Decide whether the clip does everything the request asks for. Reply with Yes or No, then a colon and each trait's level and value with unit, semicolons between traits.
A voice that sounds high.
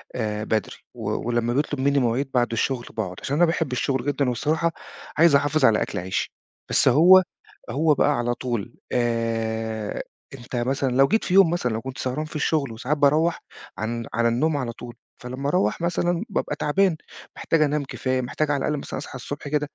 No: low, 135 Hz